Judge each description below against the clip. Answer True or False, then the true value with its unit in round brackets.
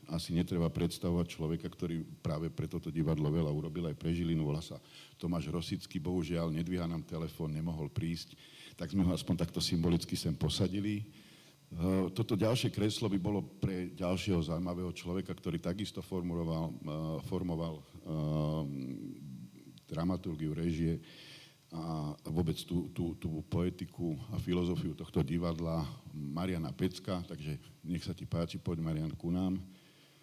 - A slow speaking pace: False (135 wpm)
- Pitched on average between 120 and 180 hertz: False (85 Hz)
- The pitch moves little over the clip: True (2.1 semitones)